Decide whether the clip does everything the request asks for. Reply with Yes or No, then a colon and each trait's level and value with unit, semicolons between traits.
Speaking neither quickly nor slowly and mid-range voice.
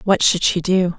No: fast, 245 wpm; medium, 180 Hz